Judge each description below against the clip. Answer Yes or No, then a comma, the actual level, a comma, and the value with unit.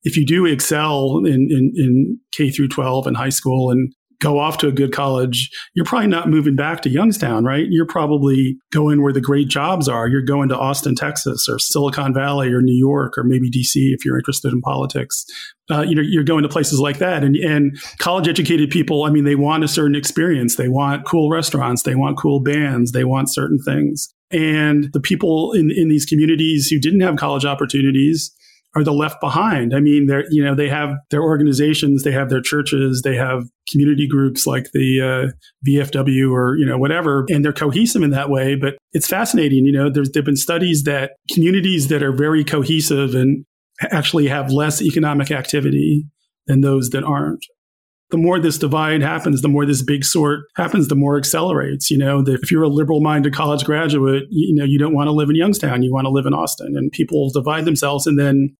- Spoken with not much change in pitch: Yes, narrow, 2.0 semitones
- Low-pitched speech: No, medium, 145 Hz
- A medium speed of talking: No, fast, 210 wpm